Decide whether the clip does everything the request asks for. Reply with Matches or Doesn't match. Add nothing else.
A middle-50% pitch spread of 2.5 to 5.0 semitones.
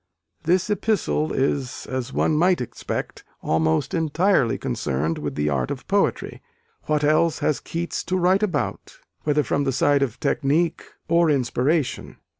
Doesn't match